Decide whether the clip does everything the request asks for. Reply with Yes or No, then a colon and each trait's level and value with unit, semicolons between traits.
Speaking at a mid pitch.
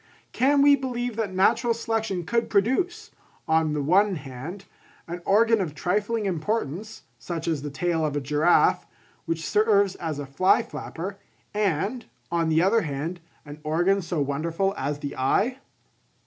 Yes: medium, 180 Hz